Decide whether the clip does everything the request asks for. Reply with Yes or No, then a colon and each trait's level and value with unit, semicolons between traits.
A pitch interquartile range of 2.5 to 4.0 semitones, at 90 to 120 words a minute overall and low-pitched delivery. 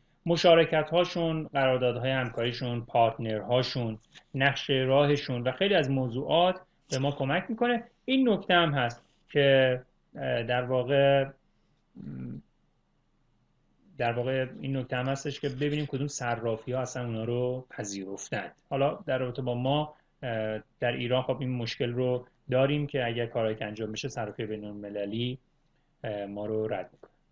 No: average, 3.4 semitones; average, 140 wpm; low, 130 Hz